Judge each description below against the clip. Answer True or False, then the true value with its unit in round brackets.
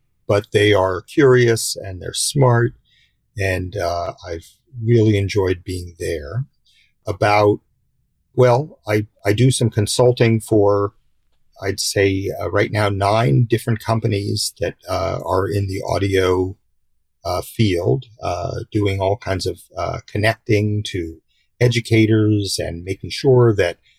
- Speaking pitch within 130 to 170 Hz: False (105 Hz)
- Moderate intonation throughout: True (3.4 semitones)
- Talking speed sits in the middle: False (130 wpm)